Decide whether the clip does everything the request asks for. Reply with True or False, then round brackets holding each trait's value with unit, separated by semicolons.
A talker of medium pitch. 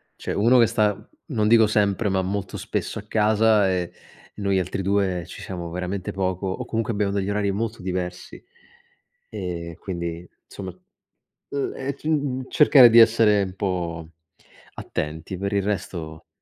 False (100 Hz)